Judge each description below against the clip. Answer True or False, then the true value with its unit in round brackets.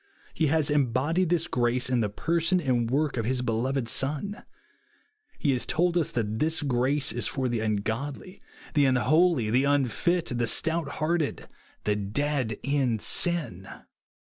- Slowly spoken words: False (150 wpm)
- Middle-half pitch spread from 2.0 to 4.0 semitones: False (4.9 semitones)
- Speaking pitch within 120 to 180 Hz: True (135 Hz)